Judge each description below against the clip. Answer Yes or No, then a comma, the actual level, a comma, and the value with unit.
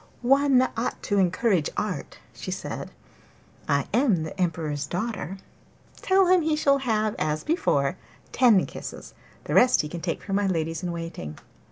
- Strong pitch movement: Yes, wide, 7.4 semitones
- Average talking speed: Yes, average, 160 wpm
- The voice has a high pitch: Yes, high, 195 Hz